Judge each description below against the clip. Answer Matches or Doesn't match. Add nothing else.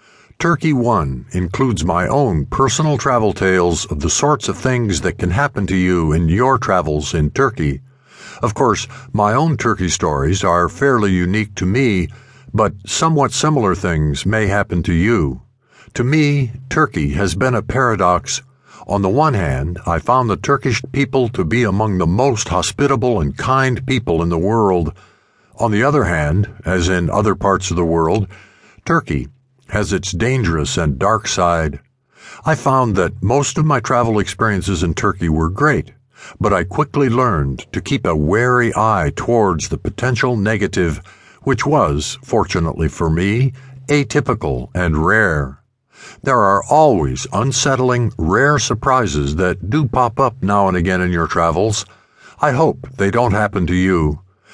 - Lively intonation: Matches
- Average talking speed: Matches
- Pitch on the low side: Matches